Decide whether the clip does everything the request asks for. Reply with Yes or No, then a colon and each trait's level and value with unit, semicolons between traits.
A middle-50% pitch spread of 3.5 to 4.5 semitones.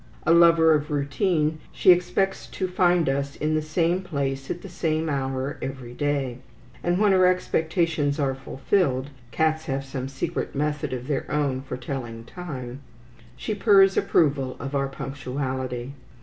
Yes: average, 3.9 semitones